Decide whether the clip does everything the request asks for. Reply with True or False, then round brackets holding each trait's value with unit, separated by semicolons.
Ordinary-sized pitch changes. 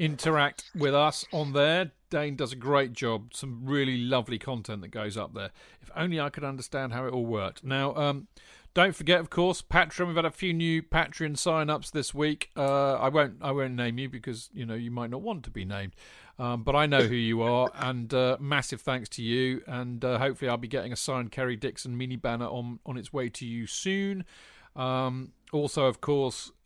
True (3.3 semitones)